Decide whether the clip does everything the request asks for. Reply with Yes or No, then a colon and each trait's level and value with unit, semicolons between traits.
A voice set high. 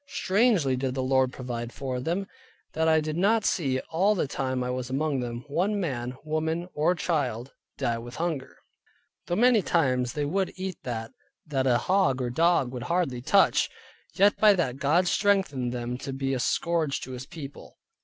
No: medium, 140 Hz